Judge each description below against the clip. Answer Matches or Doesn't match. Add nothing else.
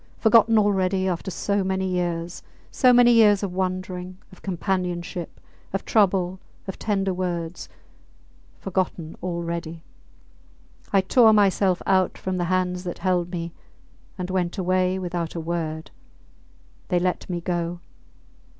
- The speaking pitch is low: Doesn't match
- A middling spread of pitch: Doesn't match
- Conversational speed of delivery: Doesn't match